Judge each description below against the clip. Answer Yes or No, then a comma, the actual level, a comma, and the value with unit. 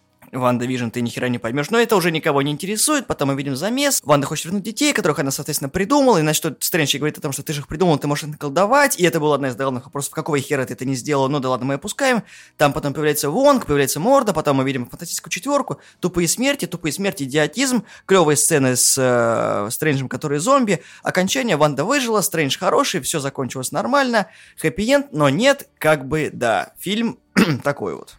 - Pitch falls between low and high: Yes, medium, 155 Hz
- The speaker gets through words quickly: Yes, fast, 205 wpm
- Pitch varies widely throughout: Yes, wide, 6.5 semitones